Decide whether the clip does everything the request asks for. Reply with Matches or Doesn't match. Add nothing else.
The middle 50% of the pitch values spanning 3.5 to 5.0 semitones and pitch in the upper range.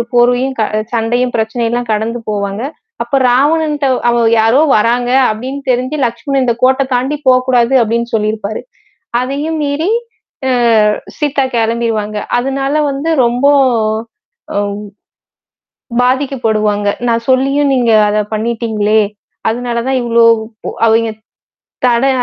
Doesn't match